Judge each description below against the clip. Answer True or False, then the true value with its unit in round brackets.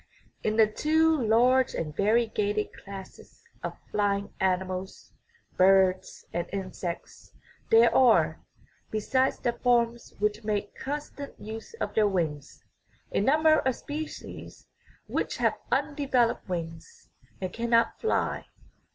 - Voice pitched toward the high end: True (215 Hz)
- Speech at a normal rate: False (115 wpm)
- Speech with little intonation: False (5.1 semitones)